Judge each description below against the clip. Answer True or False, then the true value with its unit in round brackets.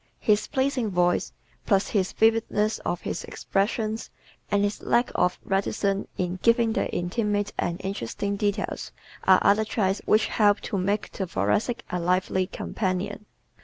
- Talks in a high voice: True (205 Hz)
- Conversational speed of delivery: True (145 wpm)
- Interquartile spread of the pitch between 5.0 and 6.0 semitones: False (2.7 semitones)